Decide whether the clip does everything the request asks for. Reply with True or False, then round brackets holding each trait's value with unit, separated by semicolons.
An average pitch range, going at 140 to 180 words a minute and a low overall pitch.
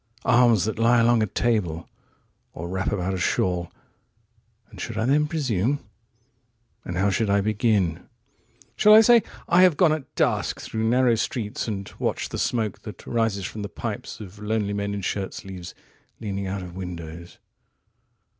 True (4.0 semitones; 155 wpm; 105 Hz)